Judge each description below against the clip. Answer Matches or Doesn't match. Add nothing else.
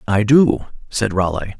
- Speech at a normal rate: Matches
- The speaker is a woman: Doesn't match